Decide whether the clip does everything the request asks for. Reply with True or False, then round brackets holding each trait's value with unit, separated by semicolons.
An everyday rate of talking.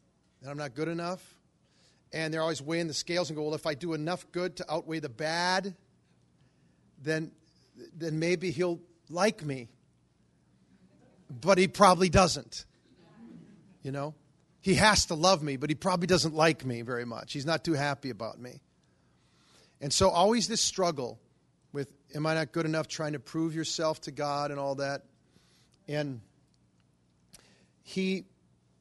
True (160 wpm)